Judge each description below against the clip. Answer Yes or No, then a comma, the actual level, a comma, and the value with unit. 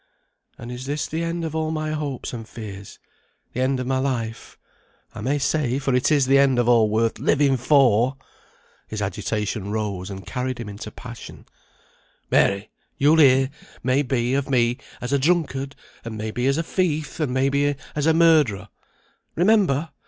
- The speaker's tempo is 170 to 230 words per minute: Yes, average, 180 wpm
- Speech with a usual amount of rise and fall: Yes, average, 4.0 semitones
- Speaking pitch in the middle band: No, low, 130 Hz